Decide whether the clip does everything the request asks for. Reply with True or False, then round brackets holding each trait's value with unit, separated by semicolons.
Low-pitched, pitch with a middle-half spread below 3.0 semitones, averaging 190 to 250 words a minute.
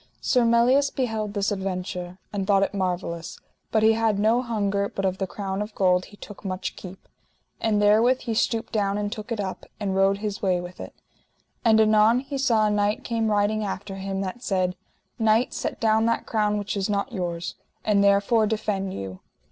False (205 Hz; 2.4 semitones; 195 wpm)